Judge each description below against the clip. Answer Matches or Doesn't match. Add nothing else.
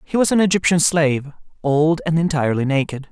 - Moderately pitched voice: Matches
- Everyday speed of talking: Matches